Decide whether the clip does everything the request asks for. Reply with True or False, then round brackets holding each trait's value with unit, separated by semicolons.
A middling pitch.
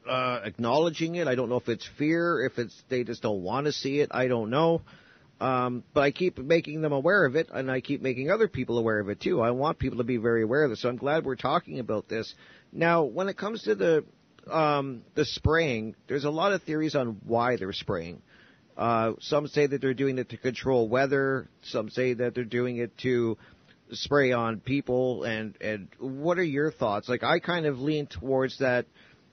False (130 Hz)